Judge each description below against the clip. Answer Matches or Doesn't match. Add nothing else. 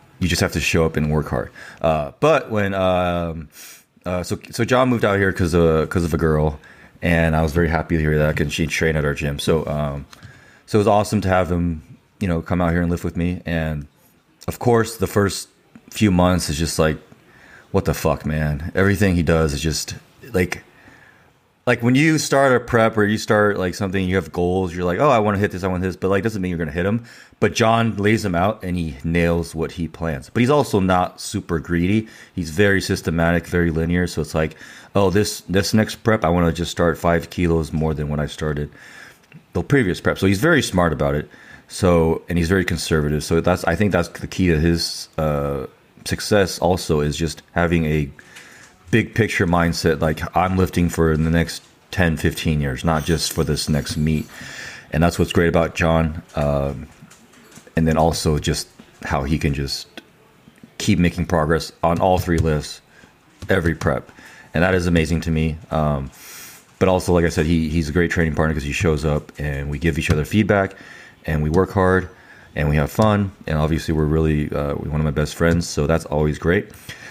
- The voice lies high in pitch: Doesn't match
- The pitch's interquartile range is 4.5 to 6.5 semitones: Doesn't match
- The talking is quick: Matches